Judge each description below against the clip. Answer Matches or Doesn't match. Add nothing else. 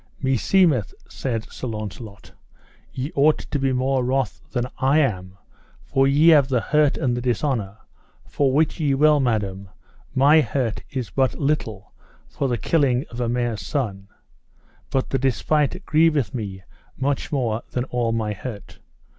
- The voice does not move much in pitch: Doesn't match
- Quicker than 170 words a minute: Doesn't match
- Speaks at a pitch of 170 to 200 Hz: Doesn't match